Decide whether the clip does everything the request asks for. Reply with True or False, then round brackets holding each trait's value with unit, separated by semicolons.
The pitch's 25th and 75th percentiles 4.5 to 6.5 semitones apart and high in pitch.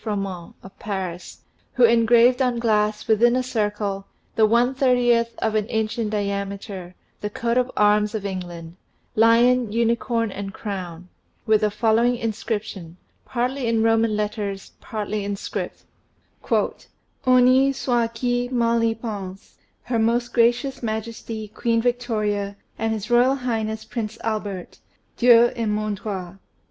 False (2.5 semitones; 220 Hz)